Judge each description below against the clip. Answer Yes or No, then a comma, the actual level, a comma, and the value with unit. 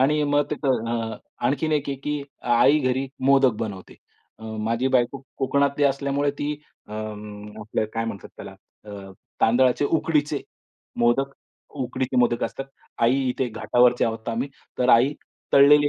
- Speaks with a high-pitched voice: No, low, 130 Hz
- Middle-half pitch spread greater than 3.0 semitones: Yes, average, 3.7 semitones